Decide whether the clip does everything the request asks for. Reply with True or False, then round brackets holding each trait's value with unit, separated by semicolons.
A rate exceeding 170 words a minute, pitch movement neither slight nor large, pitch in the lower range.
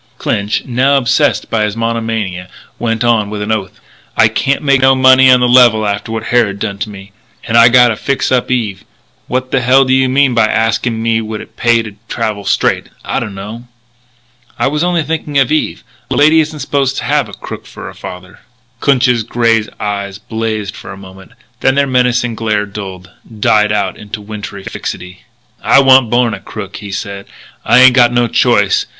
True (195 wpm; 3.8 semitones; 115 Hz)